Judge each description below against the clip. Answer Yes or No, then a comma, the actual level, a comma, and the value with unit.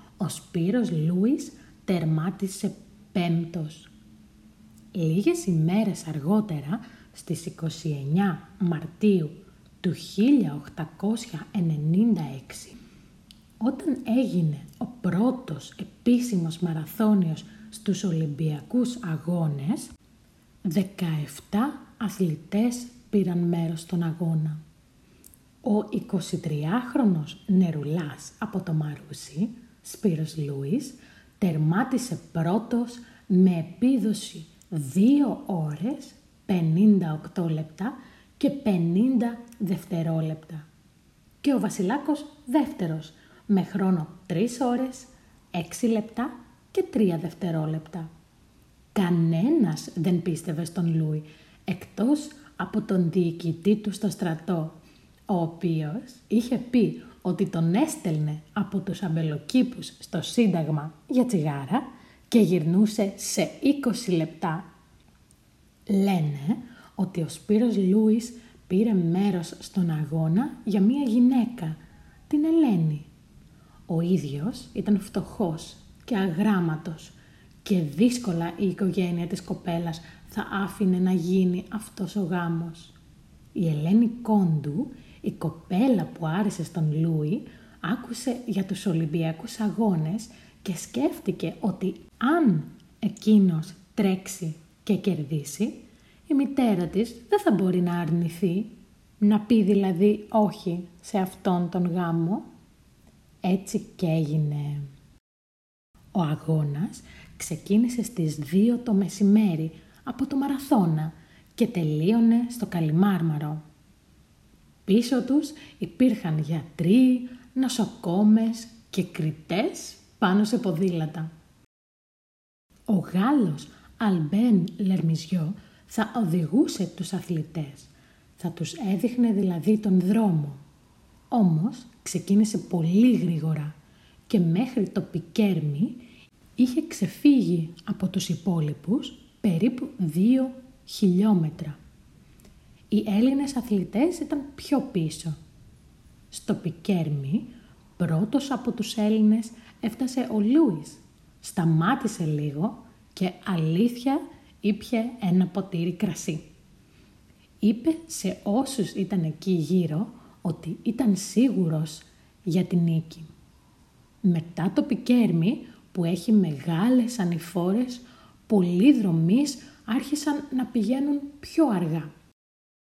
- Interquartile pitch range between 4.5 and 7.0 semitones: Yes, average, 5.3 semitones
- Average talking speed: No, slow, 95 wpm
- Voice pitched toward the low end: No, high, 195 Hz